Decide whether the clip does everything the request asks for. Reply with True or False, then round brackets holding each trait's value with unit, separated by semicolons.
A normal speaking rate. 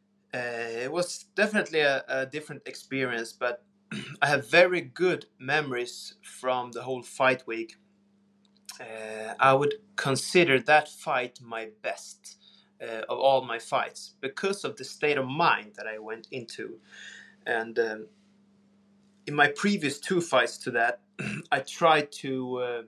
True (145 wpm)